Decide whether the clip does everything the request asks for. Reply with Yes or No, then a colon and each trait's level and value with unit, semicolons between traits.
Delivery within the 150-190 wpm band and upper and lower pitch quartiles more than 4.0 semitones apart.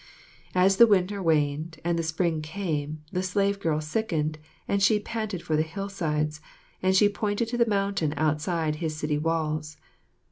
Yes: average, 165 wpm; average, 4.4 semitones